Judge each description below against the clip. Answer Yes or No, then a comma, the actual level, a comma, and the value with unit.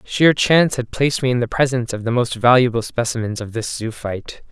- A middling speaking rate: No, fast, 215 wpm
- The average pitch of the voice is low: Yes, low, 120 Hz